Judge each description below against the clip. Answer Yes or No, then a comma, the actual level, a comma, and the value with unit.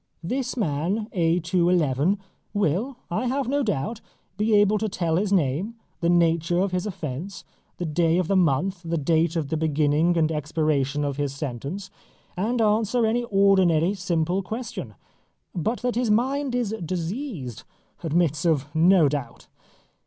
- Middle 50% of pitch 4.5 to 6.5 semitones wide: Yes, average, 5.0 semitones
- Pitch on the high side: No, medium, 175 Hz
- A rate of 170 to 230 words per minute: No, average, 155 wpm